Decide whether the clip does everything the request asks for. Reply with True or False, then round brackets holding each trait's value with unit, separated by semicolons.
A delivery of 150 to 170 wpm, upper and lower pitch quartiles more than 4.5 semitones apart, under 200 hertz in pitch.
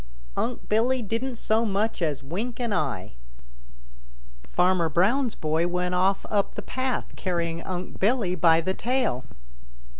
False (140 wpm; 5.4 semitones; 190 Hz)